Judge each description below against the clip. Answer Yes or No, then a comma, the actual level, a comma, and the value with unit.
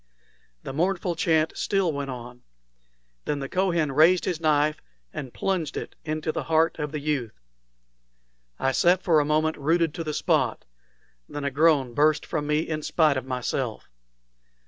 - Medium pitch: Yes, medium, 155 Hz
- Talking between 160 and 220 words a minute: Yes, average, 165 wpm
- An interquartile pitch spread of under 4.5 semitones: Yes, narrow, 2.6 semitones